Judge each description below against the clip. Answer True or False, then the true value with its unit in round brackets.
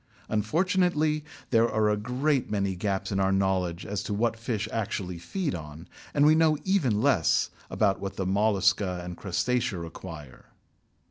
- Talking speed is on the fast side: False (155 wpm)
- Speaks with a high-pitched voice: False (105 Hz)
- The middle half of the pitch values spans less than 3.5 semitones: False (4.8 semitones)